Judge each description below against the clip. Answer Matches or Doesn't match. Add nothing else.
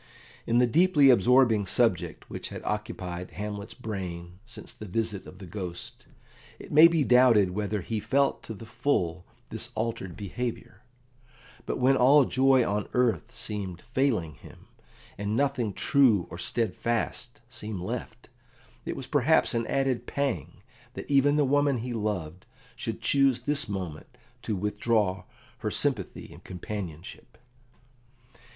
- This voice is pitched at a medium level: Doesn't match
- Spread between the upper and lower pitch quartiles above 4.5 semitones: Matches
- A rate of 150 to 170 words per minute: Doesn't match